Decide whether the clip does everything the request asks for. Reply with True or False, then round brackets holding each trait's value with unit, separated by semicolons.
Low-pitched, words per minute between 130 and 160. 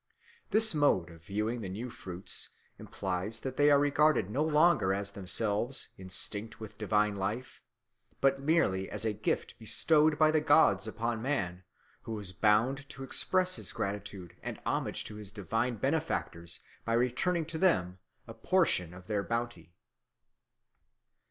True (115 Hz; 150 wpm)